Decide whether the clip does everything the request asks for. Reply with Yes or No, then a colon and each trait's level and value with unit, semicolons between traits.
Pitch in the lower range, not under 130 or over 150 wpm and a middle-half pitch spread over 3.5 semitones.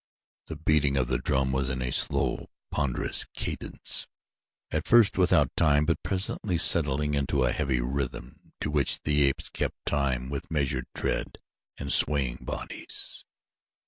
No: very low, 70 Hz; average, 145 wpm; narrow, 2.4 semitones